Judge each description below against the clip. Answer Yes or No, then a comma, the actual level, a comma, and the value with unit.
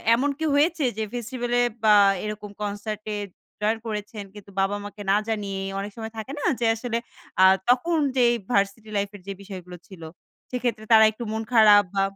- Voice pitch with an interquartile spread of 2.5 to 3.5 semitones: Yes, average, 2.8 semitones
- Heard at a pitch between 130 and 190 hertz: No, high, 215 Hz